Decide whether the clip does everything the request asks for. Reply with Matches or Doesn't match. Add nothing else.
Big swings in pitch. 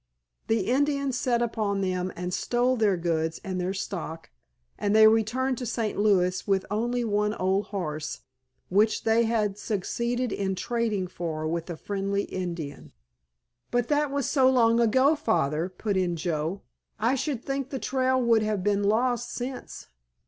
Doesn't match